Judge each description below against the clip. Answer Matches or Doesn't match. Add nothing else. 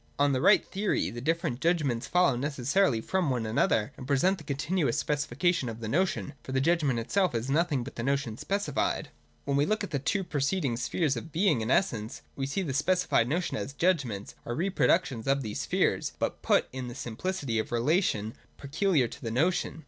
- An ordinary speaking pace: Doesn't match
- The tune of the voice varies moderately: Doesn't match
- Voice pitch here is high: Doesn't match